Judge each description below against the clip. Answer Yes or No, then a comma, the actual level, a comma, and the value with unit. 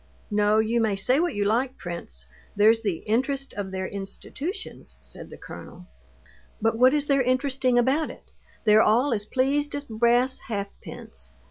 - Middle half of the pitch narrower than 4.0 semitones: No, average, 4.4 semitones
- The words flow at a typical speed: Yes, average, 160 wpm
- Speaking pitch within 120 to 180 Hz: No, high, 230 Hz